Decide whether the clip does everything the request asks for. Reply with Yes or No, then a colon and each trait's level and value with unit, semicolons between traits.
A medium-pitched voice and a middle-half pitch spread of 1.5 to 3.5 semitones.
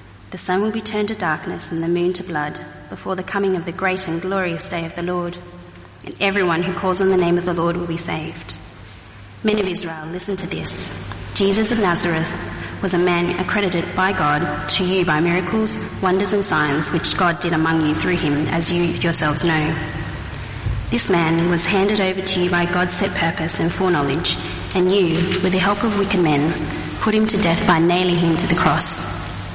Yes: medium, 175 Hz; average, 3.1 semitones